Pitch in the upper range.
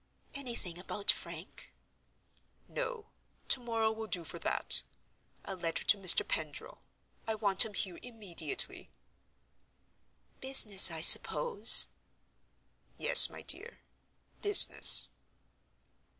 Yes: high, 210 Hz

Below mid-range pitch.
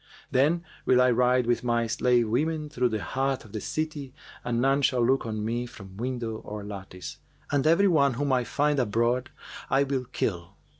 Yes: low, 125 Hz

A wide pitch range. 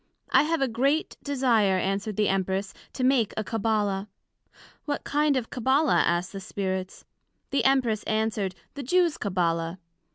Yes: wide, 5.8 semitones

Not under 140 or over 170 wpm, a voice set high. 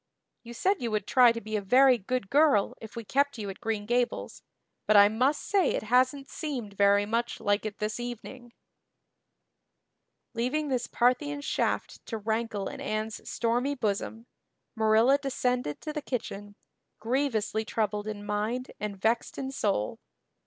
Yes: average, 160 wpm; high, 230 Hz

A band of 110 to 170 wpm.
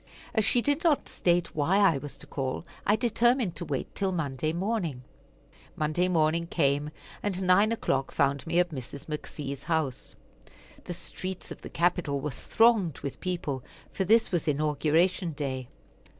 Yes: average, 160 wpm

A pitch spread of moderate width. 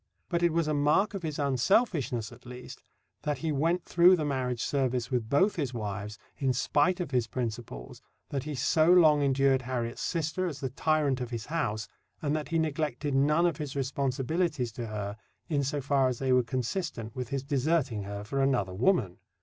Yes: average, 4.1 semitones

